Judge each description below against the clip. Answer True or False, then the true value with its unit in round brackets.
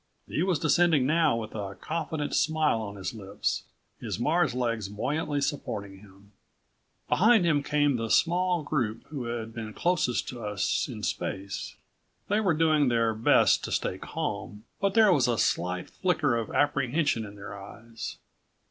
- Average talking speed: True (160 wpm)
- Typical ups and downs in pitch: False (6.5 semitones)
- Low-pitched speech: True (125 Hz)